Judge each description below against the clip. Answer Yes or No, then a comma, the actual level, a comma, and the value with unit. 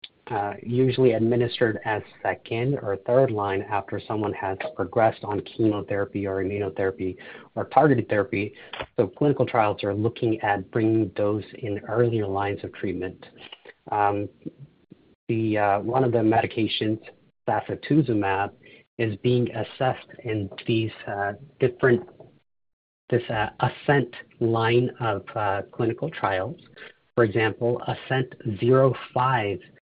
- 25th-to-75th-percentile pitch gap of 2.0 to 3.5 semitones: Yes, average, 3.1 semitones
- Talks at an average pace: No, slow, 120 wpm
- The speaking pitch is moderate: No, low, 110 Hz